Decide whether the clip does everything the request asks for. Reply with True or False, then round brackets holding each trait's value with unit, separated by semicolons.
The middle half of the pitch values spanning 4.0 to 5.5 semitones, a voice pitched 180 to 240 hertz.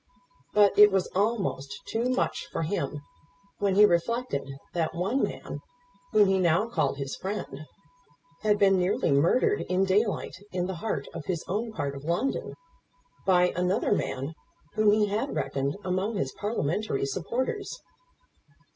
True (4.4 semitones; 190 Hz)